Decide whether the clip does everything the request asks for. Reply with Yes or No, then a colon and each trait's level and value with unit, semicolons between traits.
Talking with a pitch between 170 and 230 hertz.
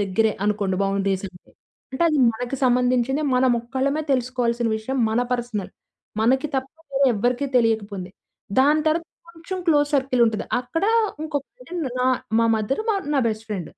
No: very high, 250 Hz